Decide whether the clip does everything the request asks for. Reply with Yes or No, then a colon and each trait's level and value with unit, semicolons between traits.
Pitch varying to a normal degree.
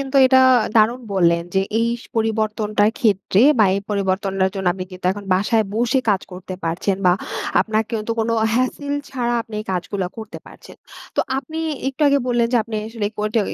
Yes: average, 3.4 semitones